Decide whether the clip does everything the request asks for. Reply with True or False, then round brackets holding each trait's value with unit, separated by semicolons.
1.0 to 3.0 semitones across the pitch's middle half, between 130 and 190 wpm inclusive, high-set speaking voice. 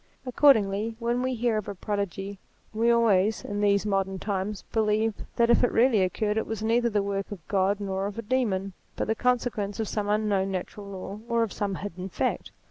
False (2.6 semitones; 205 wpm; 210 Hz)